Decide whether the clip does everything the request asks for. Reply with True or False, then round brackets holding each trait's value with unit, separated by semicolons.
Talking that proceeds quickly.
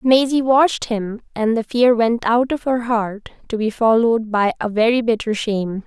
False (195 wpm)